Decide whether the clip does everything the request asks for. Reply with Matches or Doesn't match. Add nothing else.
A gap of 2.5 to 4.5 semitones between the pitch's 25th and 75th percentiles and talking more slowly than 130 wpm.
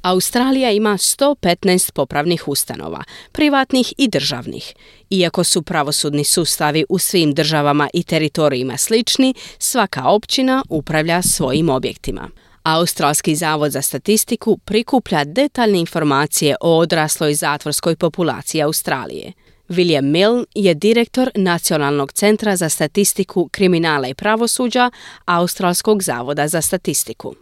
Doesn't match